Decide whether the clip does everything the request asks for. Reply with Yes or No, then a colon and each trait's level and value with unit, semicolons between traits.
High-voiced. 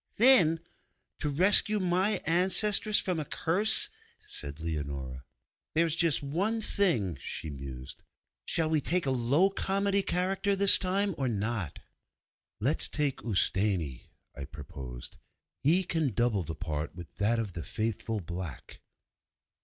No: medium, 140 Hz